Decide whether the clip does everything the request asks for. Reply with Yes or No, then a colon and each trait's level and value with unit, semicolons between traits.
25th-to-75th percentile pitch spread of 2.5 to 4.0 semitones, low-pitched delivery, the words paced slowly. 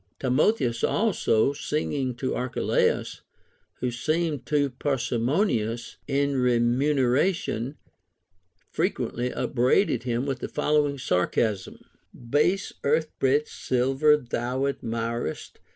Yes: average, 3.7 semitones; low, 130 Hz; slow, 95 wpm